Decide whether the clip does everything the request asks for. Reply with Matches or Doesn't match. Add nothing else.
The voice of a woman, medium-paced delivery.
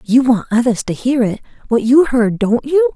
Matches